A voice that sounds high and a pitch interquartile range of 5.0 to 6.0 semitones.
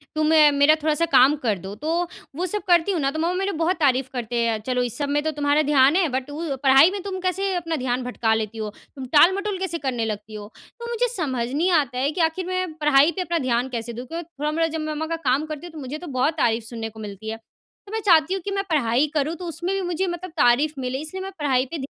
Yes: very high, 300 Hz; average, 5.3 semitones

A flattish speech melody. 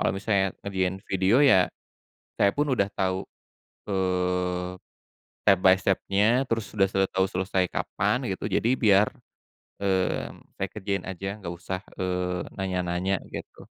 Yes: narrow, 1.4 semitones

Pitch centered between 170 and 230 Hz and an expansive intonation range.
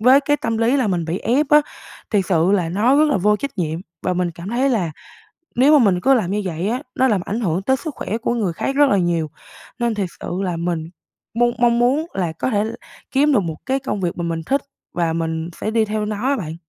Yes: high, 210 Hz; wide, 6.8 semitones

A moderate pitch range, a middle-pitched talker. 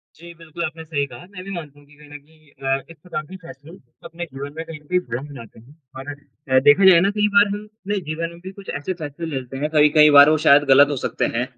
Yes: average, 3.3 semitones; medium, 150 Hz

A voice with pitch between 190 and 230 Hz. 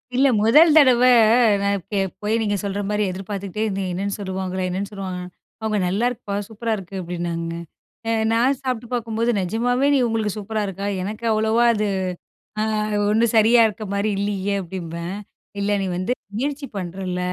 Yes: high, 205 Hz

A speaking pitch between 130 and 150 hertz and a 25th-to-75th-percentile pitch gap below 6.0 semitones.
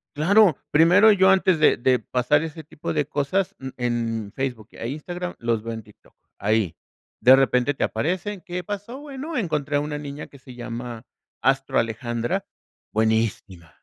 No: medium, 140 Hz; wide, 7.0 semitones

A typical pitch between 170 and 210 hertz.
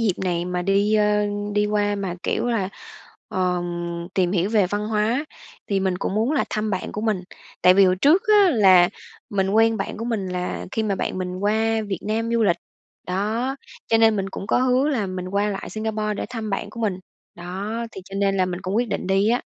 Yes: high, 205 Hz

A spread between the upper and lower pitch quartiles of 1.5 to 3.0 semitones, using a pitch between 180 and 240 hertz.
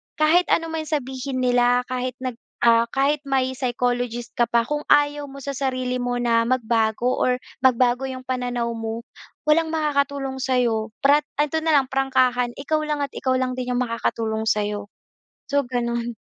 No: narrow, 2.5 semitones; very high, 255 Hz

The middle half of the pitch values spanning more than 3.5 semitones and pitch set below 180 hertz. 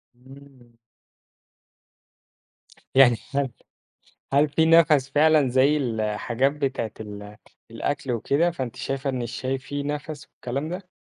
No: average, 3.2 semitones; low, 135 Hz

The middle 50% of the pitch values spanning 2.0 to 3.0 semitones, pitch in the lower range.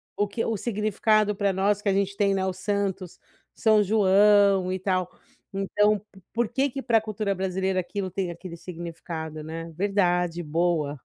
No: average, 2.7 semitones; high, 195 Hz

